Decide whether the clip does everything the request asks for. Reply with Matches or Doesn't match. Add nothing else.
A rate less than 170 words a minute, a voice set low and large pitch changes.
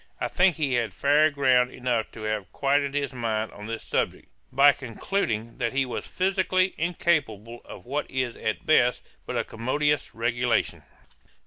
Doesn't match